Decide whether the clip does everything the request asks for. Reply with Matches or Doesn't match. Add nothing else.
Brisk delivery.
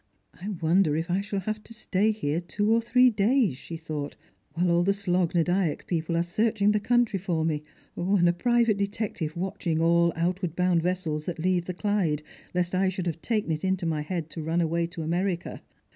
Matches